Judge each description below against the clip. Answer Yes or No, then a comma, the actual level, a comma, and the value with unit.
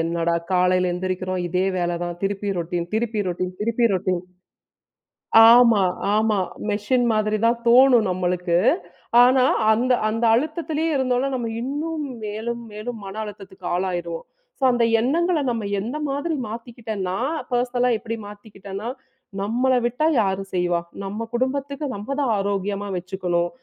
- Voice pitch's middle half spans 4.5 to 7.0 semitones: Yes, average, 4.9 semitones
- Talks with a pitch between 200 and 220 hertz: Yes, high, 215 Hz